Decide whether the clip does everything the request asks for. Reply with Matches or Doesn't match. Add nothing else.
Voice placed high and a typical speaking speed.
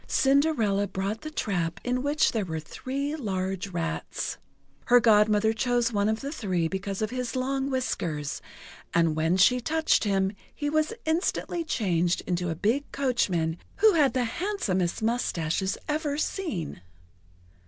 Matches